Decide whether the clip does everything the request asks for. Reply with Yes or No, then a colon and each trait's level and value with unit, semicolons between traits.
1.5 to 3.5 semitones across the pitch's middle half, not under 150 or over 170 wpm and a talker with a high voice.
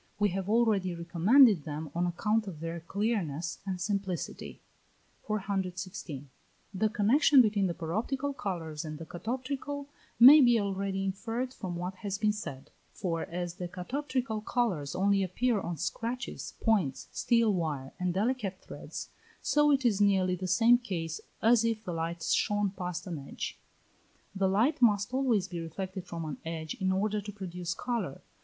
No: average, 4.5 semitones; average, 160 wpm; high, 195 Hz